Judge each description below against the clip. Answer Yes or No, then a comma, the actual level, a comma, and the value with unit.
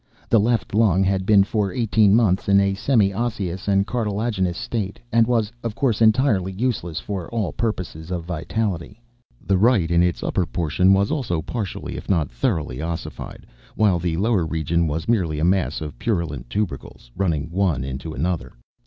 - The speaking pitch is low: Yes, very low, 95 Hz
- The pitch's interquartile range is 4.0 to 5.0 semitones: Yes, average, 4.4 semitones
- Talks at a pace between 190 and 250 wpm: No, average, 170 wpm